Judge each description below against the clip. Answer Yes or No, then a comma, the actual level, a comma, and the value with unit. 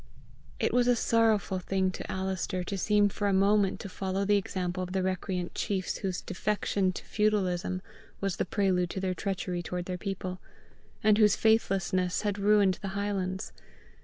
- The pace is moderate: Yes, average, 170 wpm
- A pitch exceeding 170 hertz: Yes, high, 190 Hz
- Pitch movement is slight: Yes, narrow, 1.8 semitones